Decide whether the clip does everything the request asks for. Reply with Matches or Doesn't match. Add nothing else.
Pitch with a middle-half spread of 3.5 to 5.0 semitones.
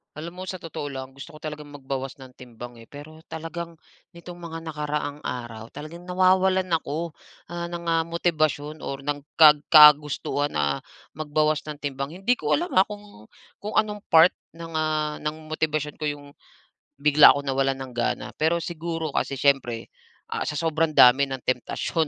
Doesn't match